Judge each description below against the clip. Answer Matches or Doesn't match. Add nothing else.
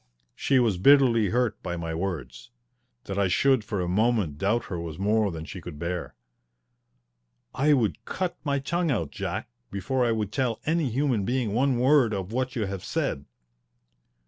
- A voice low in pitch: Matches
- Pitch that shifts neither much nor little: Doesn't match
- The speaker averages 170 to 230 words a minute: Matches